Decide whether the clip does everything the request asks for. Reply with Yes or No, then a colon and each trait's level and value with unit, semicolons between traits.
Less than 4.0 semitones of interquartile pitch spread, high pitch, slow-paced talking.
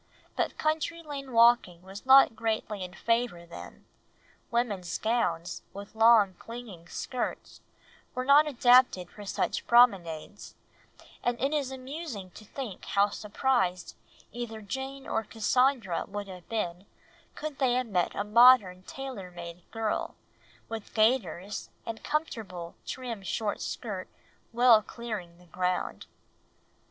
No: average, 5.1 semitones; high, 225 Hz; slow, 125 wpm